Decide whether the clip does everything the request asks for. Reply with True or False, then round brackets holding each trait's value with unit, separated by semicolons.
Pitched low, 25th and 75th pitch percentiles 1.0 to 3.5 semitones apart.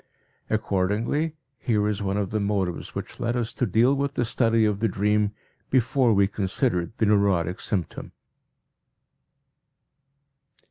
True (105 Hz; 3.0 semitones)